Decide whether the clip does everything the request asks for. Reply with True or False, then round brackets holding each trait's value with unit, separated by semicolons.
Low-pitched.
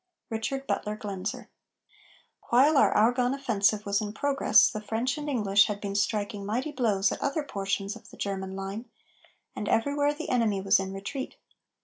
False (215 Hz)